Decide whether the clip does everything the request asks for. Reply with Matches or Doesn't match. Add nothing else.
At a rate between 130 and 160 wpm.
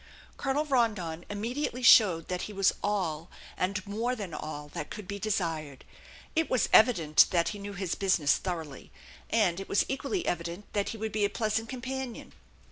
Doesn't match